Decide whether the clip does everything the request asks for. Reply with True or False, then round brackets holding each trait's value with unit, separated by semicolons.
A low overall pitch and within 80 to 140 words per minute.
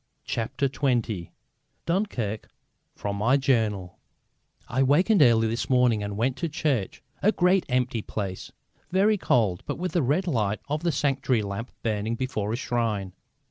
False (125 Hz; 150 wpm)